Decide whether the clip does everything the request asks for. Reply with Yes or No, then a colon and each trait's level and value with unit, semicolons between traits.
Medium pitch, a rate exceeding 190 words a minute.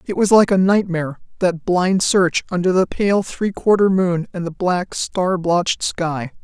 No: medium, 180 Hz; average, 185 wpm